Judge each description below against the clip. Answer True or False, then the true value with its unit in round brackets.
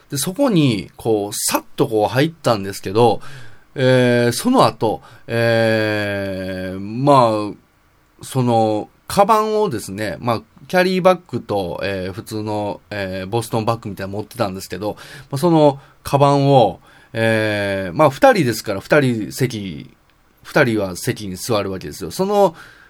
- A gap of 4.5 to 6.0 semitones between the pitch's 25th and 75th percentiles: True (5.6 semitones)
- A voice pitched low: True (115 Hz)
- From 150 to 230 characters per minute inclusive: False (285 characters per minute)